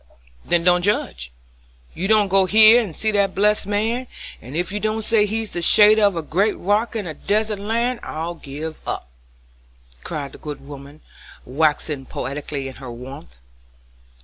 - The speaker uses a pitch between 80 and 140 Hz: No, medium, 185 Hz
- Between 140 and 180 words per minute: Yes, average, 165 wpm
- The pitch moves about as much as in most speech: No, wide, 6.3 semitones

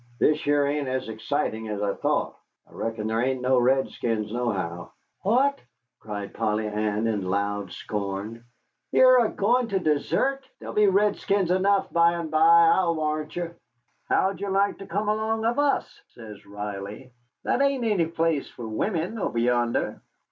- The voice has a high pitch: No, medium, 145 Hz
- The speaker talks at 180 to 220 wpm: No, average, 160 wpm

